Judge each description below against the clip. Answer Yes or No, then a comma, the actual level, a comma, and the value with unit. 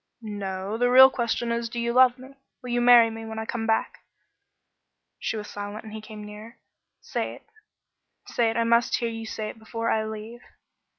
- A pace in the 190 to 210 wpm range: Yes, average, 200 wpm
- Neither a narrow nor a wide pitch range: No, narrow, 1.6 semitones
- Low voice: No, high, 225 Hz